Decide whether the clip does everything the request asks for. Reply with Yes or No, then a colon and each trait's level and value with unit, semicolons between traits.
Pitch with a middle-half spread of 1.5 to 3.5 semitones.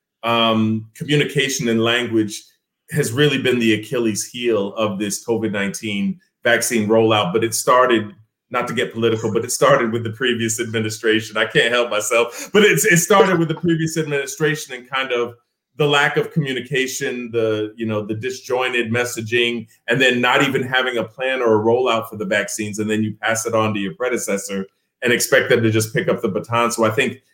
Yes: average, 2.9 semitones